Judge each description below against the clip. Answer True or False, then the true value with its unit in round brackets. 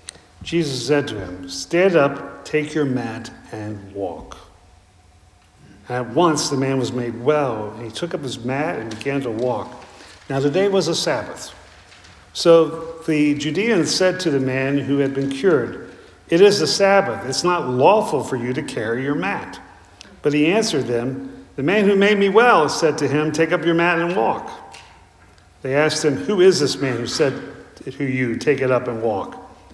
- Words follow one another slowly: False (190 wpm)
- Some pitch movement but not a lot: False (6.8 semitones)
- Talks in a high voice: False (135 Hz)